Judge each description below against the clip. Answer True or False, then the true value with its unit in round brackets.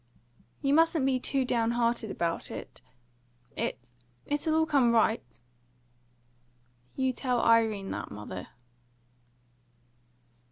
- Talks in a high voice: True (230 Hz)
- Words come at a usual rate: False (110 wpm)